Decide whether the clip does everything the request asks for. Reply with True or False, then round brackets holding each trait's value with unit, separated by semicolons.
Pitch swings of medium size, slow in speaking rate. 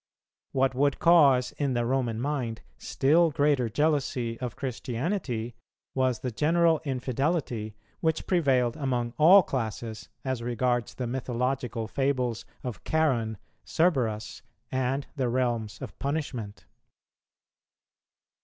True (3.3 semitones; 110 wpm)